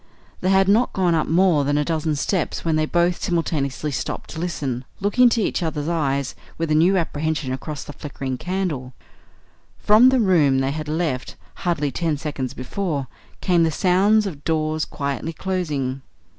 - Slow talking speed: No, average, 175 wpm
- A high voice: No, medium, 160 Hz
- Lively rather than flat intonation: No, average, 4.0 semitones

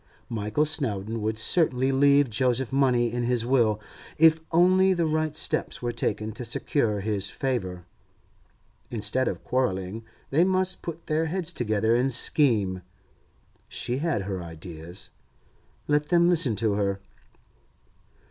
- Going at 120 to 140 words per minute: Yes, slow, 135 wpm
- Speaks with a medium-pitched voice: No, low, 125 Hz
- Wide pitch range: Yes, wide, 6.2 semitones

